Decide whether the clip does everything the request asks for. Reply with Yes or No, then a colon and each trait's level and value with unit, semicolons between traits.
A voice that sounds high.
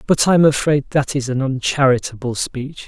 No: low, 135 Hz